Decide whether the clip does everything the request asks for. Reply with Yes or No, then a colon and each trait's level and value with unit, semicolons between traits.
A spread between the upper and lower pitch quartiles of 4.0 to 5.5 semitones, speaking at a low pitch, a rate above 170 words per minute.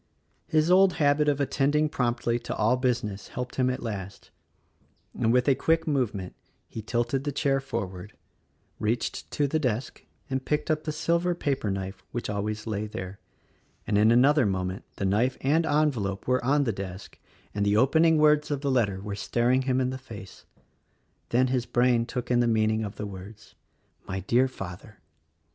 Yes: average, 5.1 semitones; low, 120 Hz; average, 185 wpm